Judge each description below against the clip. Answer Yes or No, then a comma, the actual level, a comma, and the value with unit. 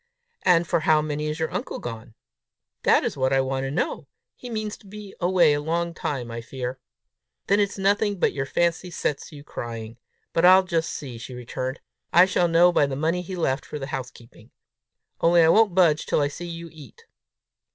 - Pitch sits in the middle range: Yes, medium, 160 Hz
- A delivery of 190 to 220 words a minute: Yes, fast, 205 wpm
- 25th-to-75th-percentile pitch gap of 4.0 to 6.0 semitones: Yes, average, 4.9 semitones